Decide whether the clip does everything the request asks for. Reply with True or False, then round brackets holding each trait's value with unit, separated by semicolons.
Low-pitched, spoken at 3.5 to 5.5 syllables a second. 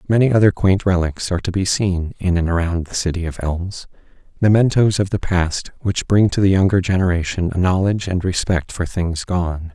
True (90 Hz; 5.3 syllables/s)